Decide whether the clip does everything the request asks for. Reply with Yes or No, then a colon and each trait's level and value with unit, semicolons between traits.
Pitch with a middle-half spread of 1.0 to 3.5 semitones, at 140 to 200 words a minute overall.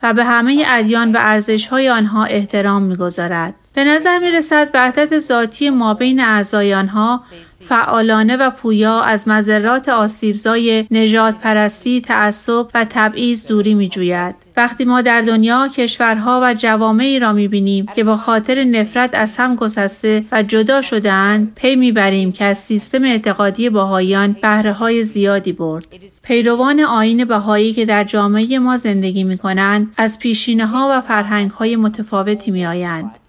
Yes: average, 2.7 semitones; fast, 155 wpm